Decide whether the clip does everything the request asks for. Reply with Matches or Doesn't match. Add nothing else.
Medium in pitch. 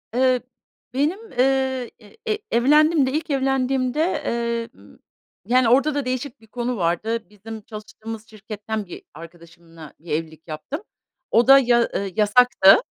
Doesn't match